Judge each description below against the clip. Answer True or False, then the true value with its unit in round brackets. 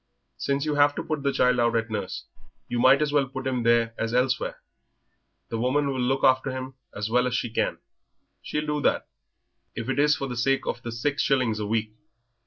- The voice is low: True (130 Hz)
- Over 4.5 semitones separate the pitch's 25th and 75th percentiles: False (2.9 semitones)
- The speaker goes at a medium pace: False (215 wpm)